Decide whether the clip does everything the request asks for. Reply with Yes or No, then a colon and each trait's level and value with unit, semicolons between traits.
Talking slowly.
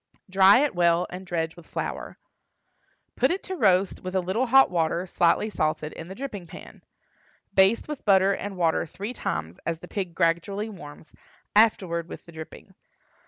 No: average, 170 wpm